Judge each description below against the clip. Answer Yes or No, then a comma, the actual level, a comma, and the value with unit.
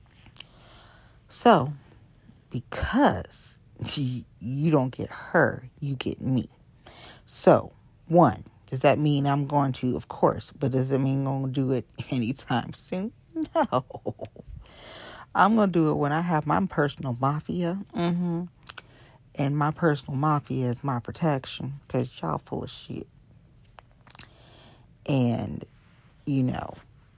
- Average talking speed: No, slow, 130 wpm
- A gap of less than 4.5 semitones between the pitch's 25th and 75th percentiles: Yes, average, 3.2 semitones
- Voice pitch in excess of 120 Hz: Yes, low, 135 Hz